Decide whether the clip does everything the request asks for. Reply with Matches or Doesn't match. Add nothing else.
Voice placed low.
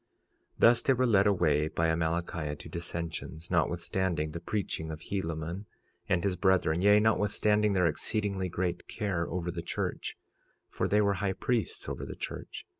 Matches